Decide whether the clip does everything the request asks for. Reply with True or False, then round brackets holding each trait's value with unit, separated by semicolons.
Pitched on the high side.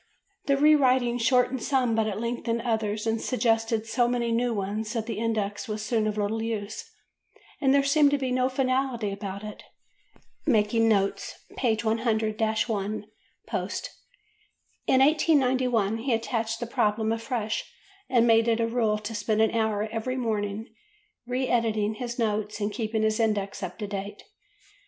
True (225 Hz)